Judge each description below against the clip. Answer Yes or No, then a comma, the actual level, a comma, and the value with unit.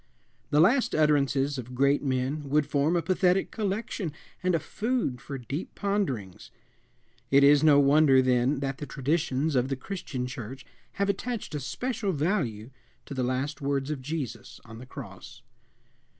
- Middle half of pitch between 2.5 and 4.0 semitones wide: No, average, 4.6 semitones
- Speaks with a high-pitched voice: No, medium, 145 Hz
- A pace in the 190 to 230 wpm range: No, average, 160 wpm